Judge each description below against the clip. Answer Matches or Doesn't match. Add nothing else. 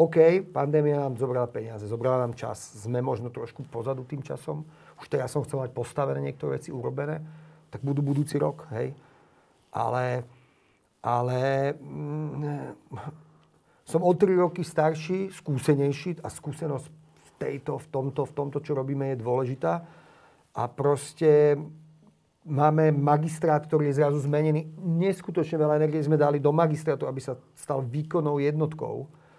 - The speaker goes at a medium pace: Matches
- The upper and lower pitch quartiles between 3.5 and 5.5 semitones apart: Doesn't match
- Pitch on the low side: Doesn't match